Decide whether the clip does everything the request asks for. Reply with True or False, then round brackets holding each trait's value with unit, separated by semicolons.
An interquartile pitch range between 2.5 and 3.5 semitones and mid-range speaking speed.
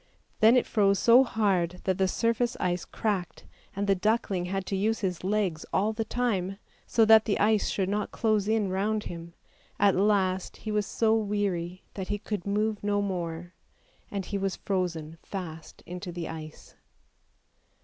True (2.9 semitones; 170 wpm)